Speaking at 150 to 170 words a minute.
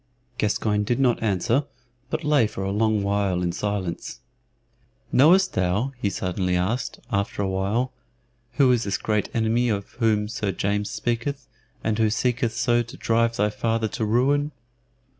Yes: average, 160 wpm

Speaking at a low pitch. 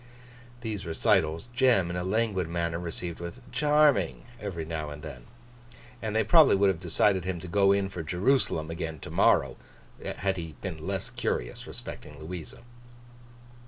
Yes: very low, 90 Hz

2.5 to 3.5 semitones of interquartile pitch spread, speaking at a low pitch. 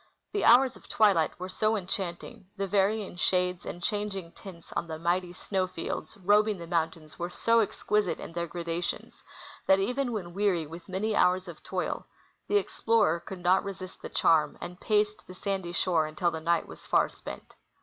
No: average, 3.2 semitones; medium, 185 Hz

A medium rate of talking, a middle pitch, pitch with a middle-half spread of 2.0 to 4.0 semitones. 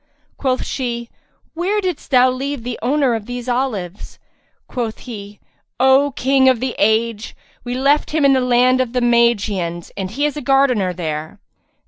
No: average, 165 wpm; high, 245 Hz; average, 3.6 semitones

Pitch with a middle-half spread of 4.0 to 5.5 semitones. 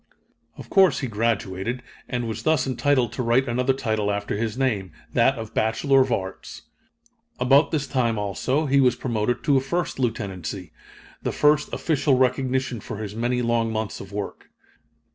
No: average, 3.5 semitones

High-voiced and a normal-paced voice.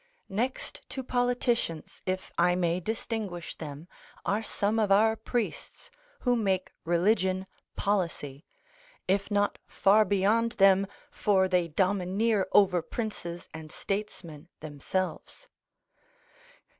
No: high, 195 Hz; slow, 105 wpm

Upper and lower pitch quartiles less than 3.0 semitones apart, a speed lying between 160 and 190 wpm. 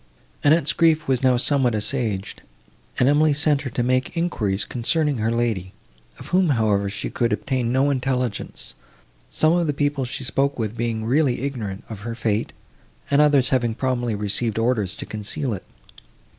No: average, 4.2 semitones; average, 170 wpm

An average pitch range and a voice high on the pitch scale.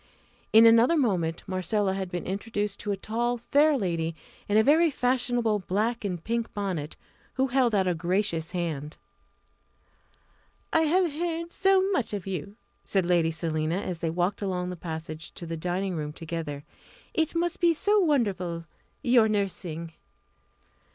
No: wide, 6.2 semitones; high, 200 Hz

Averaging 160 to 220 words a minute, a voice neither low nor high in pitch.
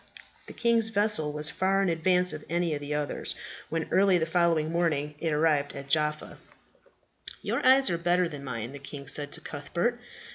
Yes: average, 185 wpm; medium, 160 Hz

